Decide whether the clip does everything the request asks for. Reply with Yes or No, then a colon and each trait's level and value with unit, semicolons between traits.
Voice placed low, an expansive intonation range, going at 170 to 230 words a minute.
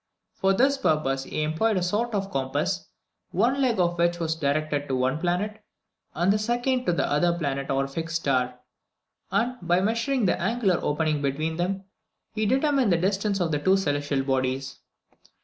No: medium, 175 Hz; wide, 6.3 semitones; average, 175 wpm